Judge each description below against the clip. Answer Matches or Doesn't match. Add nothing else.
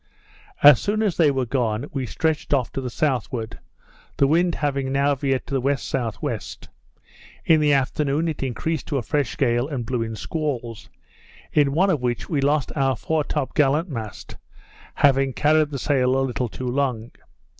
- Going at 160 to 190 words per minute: Matches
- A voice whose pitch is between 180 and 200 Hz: Doesn't match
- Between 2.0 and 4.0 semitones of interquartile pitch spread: Matches